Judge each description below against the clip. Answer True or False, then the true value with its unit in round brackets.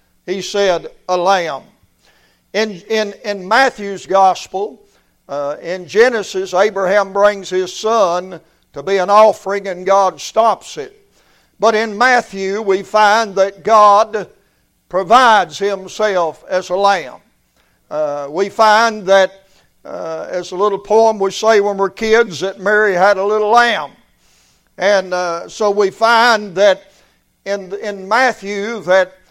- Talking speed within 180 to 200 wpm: False (135 wpm)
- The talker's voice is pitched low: False (200 Hz)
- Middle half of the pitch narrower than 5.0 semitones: True (2.5 semitones)